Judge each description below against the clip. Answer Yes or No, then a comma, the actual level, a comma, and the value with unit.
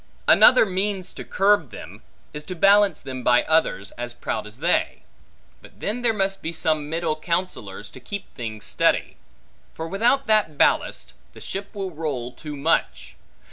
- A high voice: No, medium, 160 Hz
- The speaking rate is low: No, average, 165 wpm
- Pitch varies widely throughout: Yes, wide, 7.2 semitones